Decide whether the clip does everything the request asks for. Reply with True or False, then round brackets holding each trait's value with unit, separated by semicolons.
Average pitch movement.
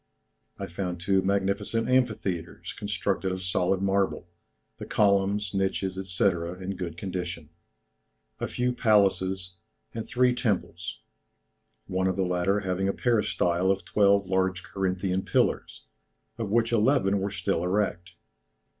False (2.0 semitones)